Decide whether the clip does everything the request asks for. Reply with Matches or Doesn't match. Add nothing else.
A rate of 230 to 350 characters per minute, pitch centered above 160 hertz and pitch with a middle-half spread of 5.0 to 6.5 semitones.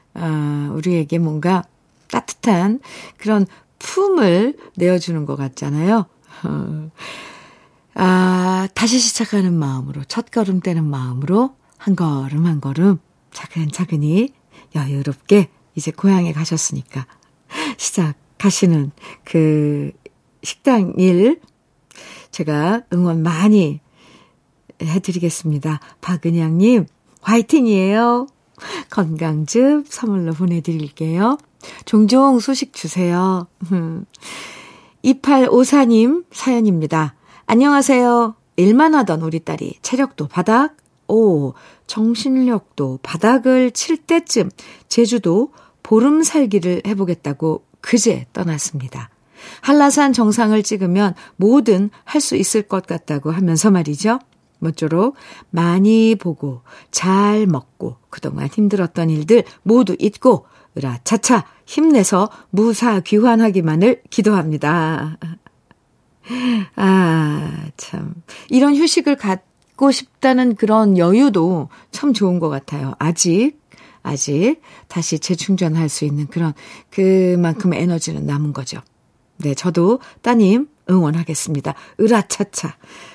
Doesn't match